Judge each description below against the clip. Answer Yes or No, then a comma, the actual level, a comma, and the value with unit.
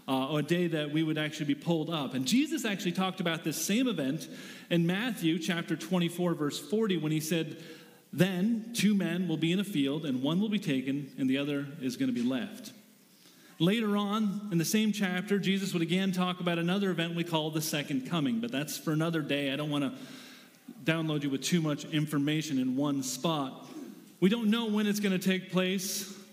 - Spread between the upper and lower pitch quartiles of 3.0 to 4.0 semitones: No, average, 5.0 semitones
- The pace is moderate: No, fast, 215 wpm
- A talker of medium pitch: Yes, medium, 175 Hz